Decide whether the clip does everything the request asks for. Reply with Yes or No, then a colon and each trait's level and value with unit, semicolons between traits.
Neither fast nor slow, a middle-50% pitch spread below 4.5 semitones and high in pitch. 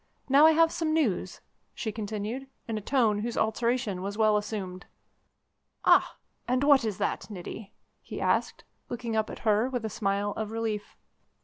Yes: average, 170 wpm; average, 3.3 semitones; high, 220 Hz